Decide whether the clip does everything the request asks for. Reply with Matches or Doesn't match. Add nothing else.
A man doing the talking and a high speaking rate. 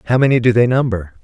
Matches